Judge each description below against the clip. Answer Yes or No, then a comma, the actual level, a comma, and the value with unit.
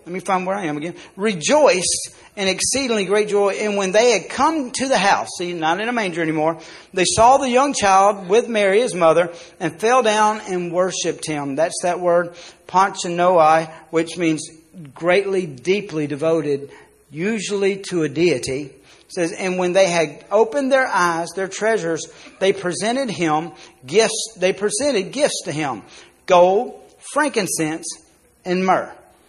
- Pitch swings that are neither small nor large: Yes, average, 4.4 semitones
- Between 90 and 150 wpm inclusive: No, average, 160 wpm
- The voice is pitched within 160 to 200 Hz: Yes, medium, 185 Hz